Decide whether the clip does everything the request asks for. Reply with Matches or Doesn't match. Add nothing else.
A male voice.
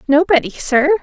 Doesn't match